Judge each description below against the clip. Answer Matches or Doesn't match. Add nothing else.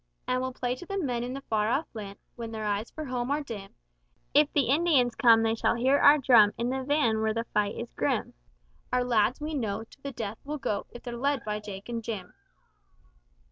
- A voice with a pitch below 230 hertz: Doesn't match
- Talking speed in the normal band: Doesn't match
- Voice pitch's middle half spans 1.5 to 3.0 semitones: Doesn't match